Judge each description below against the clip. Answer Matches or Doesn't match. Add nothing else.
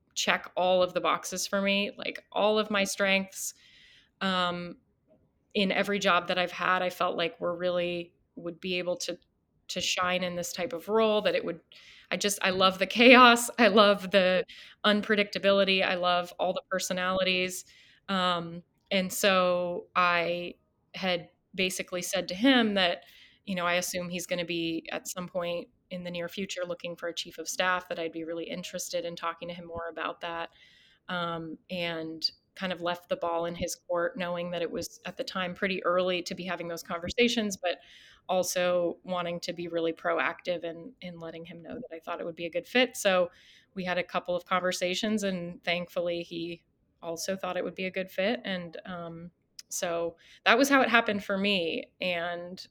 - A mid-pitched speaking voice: Matches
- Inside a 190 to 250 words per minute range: Matches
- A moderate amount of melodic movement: Doesn't match